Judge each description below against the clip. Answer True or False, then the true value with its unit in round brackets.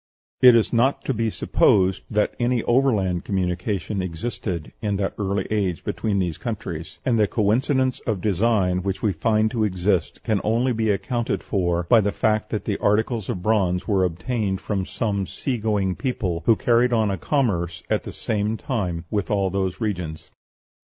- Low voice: True (105 Hz)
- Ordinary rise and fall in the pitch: True (3.6 semitones)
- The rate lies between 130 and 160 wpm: False (175 wpm)